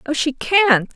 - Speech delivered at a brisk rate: No, average, 190 wpm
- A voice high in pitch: Yes, very high, 295 Hz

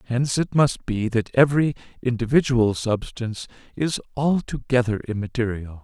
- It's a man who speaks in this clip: Yes, male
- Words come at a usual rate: No, slow, 115 wpm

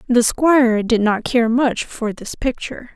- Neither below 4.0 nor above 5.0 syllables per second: Yes, 4.4 syllables/s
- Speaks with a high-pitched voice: Yes, high, 240 Hz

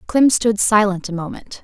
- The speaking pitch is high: Yes, high, 205 Hz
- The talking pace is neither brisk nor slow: Yes, average, 185 wpm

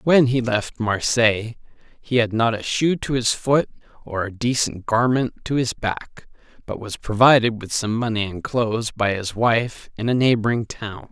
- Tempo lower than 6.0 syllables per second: Yes, 4.5 syllables/s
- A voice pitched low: Yes, low, 115 Hz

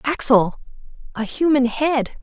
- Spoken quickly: No, slow, 110 wpm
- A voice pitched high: Yes, very high, 260 Hz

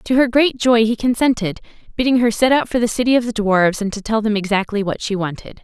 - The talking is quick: Yes, fast, 255 wpm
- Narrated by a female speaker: Yes, female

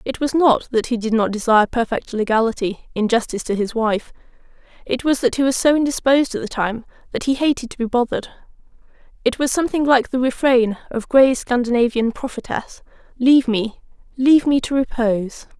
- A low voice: No, high, 245 Hz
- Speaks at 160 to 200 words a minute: Yes, average, 180 wpm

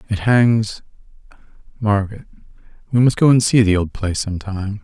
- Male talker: Yes, male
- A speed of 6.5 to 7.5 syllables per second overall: No, 5.3 syllables/s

